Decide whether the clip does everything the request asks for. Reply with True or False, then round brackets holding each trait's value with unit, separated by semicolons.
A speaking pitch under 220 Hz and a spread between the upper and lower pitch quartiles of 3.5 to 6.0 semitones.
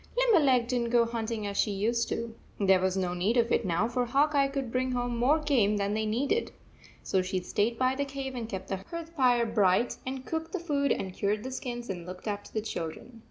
False (235 Hz; 4.6 semitones)